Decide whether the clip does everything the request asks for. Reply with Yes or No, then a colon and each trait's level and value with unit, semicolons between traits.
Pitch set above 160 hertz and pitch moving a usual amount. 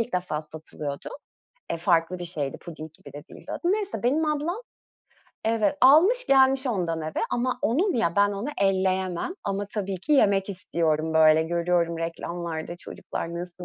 No: medium, 185 Hz; wide, 6.8 semitones